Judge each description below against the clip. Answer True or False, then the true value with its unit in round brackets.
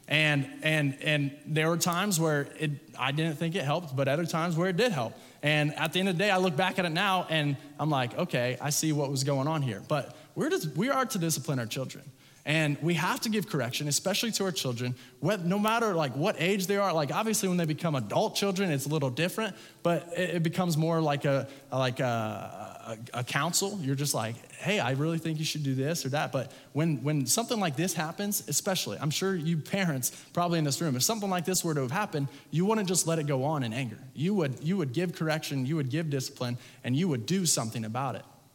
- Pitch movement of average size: True (4.6 semitones)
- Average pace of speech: False (240 wpm)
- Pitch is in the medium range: True (155 Hz)